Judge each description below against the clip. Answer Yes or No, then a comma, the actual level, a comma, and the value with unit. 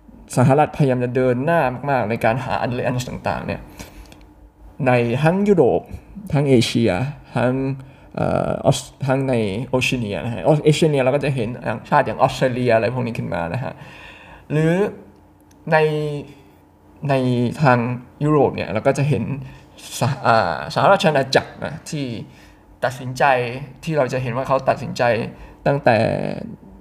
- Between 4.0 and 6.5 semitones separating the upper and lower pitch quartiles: No, average, 3.5 semitones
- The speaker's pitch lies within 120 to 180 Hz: Yes, low, 130 Hz